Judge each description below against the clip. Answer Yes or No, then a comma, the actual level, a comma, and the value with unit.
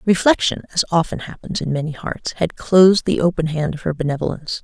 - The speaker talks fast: No, average, 195 wpm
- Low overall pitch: No, medium, 165 Hz